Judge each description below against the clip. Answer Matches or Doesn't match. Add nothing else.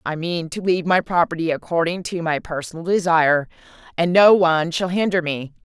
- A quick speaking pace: Doesn't match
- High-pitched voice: Doesn't match